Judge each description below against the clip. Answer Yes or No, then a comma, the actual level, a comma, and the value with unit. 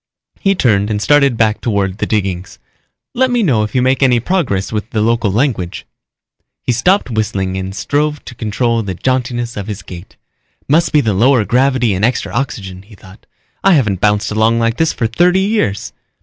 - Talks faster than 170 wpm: Yes, average, 190 wpm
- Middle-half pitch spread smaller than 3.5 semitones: No, average, 4.8 semitones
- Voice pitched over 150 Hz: No, low, 115 Hz